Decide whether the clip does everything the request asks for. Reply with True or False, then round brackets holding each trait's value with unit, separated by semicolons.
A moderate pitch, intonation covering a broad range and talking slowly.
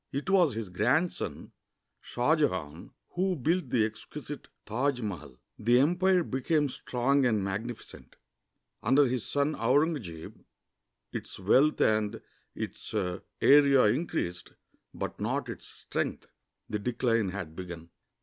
False (125 Hz; 6.2 semitones; 120 wpm)